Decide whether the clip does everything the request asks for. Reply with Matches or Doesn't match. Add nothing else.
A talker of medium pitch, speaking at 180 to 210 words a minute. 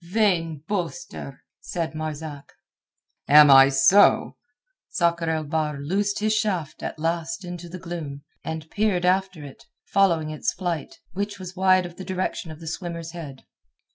Doesn't match